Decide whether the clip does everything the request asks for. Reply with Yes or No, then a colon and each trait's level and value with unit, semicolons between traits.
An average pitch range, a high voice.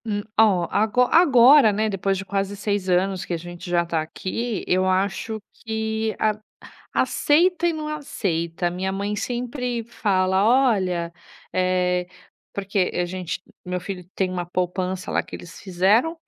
Yes: average, 3.6 semitones; high, 195 Hz